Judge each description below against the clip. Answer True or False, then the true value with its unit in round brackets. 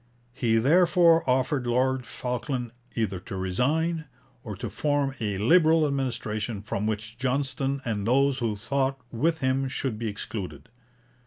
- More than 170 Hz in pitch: False (130 Hz)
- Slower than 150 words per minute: True (140 wpm)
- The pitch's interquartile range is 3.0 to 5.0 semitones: True (3.9 semitones)